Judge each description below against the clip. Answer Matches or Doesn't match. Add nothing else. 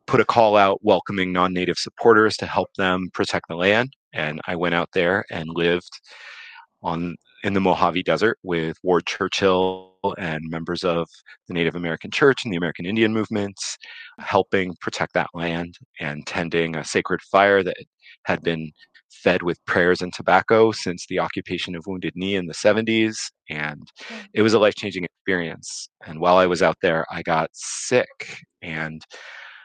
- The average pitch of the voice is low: Matches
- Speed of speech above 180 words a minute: Doesn't match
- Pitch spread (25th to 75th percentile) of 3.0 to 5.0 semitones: Doesn't match